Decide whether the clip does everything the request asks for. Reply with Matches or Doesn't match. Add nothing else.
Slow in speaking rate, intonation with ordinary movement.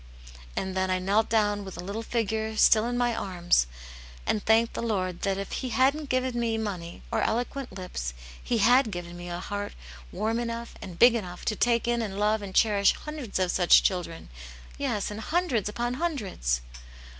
Doesn't match